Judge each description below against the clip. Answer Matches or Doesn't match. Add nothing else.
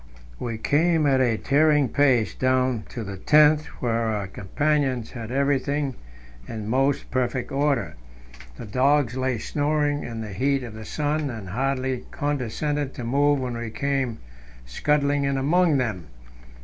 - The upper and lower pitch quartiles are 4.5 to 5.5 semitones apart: Doesn't match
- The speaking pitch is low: Matches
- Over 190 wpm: Doesn't match